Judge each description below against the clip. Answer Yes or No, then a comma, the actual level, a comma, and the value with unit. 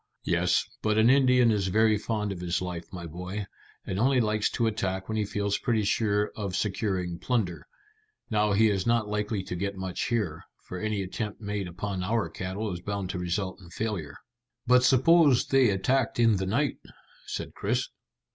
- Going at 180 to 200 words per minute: Yes, average, 185 wpm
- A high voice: No, low, 105 Hz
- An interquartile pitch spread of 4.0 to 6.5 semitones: No, average, 3.2 semitones